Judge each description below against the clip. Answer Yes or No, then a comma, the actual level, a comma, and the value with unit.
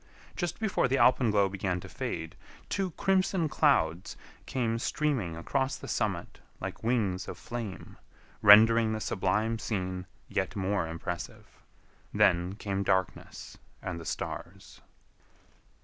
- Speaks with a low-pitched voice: Yes, low, 105 Hz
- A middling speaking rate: No, slow, 120 wpm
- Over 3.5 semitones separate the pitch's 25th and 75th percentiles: Yes, average, 5.2 semitones